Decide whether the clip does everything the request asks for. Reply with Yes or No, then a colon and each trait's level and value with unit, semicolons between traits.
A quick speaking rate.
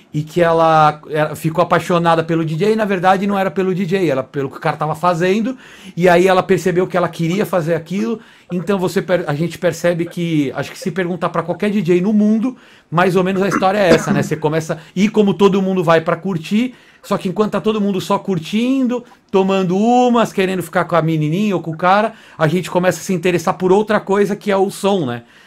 Yes: fast, 220 wpm